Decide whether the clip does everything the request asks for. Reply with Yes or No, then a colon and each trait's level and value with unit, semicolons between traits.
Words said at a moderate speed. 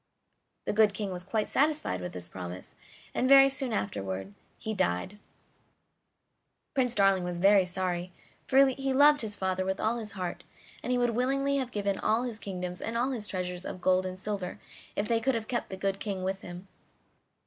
Yes: average, 190 wpm